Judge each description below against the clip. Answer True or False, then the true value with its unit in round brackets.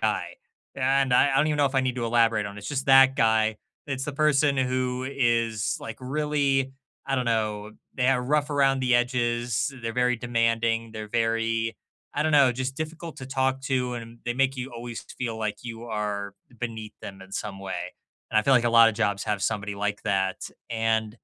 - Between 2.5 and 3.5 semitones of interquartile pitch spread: True (3.2 semitones)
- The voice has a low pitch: True (120 Hz)